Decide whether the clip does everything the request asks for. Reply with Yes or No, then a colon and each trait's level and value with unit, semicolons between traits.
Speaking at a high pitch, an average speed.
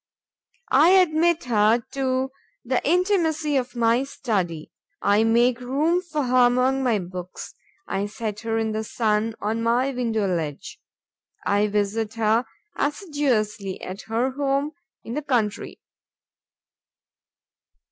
No: high, 240 Hz; slow, 125 wpm